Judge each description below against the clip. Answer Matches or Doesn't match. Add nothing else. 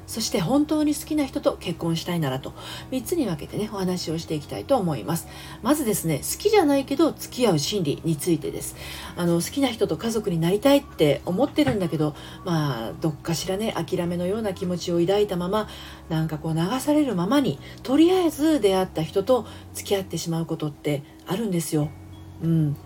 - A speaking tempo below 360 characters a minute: Doesn't match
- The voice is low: Doesn't match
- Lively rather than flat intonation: Matches